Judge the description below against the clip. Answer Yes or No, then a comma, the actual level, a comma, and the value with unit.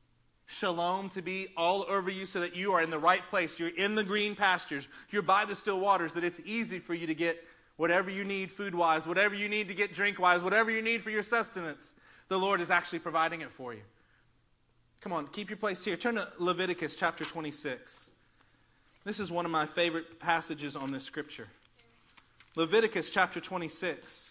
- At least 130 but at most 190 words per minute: No, average, 200 wpm